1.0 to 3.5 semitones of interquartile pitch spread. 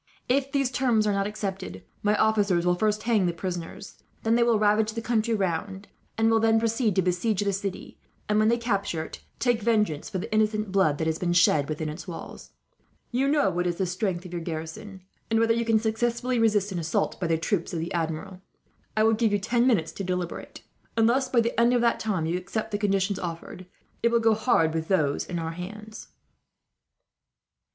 No: average, 4.2 semitones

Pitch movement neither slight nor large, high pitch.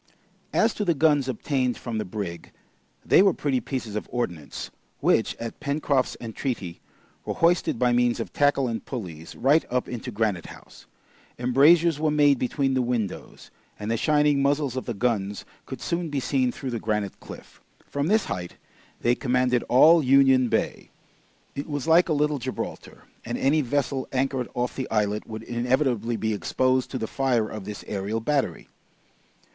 No: average, 4.0 semitones; low, 125 Hz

